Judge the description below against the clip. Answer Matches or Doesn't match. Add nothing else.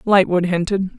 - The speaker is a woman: Matches